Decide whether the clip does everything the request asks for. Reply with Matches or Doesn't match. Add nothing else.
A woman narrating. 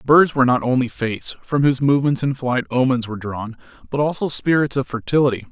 Doesn't match